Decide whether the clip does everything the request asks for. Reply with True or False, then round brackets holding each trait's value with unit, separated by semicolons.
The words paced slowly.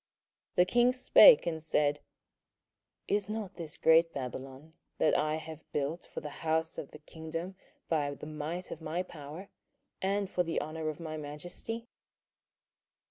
False (155 wpm)